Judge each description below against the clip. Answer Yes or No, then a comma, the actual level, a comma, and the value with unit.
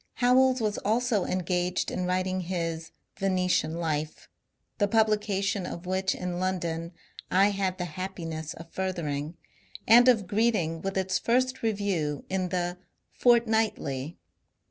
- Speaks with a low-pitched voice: No, medium, 185 Hz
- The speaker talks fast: No, average, 140 wpm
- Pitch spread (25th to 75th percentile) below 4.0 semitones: Yes, average, 3.5 semitones